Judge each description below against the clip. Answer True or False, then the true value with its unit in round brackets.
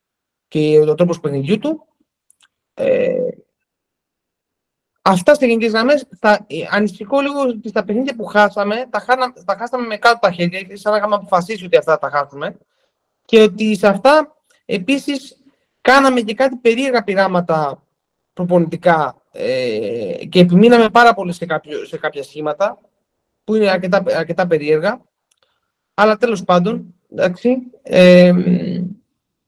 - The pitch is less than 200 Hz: False (210 Hz)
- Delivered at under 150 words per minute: True (135 wpm)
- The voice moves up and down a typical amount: False (5.9 semitones)